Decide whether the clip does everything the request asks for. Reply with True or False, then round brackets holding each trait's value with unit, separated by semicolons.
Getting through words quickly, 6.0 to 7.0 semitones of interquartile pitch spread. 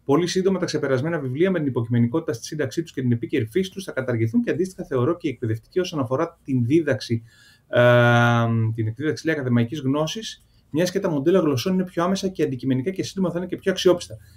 True (210 wpm; 6.4 semitones)